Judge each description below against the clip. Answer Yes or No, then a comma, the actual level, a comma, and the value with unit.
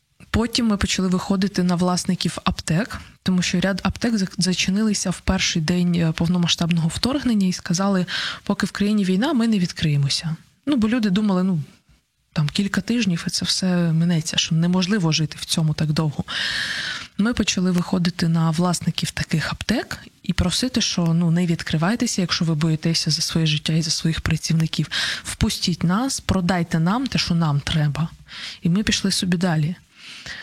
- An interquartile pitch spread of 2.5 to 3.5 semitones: Yes, average, 3.2 semitones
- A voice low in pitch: No, medium, 180 Hz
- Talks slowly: No, fast, 160 wpm